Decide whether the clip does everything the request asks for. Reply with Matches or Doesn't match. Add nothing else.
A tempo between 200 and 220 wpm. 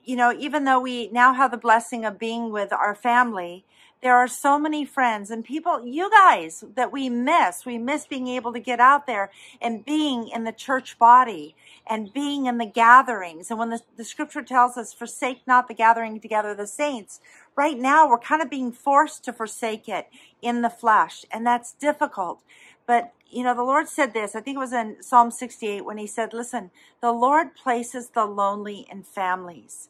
Matches